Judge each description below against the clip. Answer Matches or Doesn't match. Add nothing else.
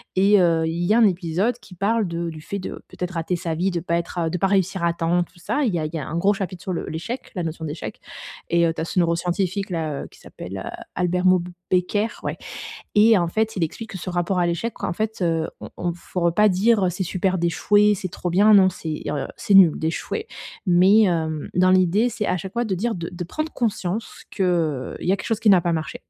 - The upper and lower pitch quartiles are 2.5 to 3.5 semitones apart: Matches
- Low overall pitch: Doesn't match